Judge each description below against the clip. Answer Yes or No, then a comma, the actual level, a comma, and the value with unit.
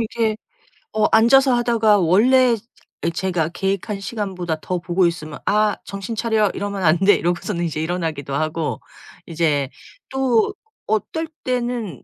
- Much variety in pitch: No, average, 4.9 semitones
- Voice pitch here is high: Yes, high, 195 Hz